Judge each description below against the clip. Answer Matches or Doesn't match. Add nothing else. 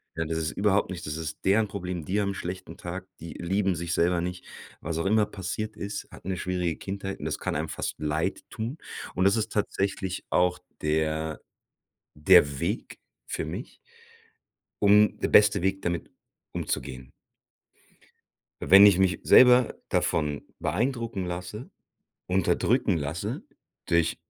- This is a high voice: Doesn't match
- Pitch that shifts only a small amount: Doesn't match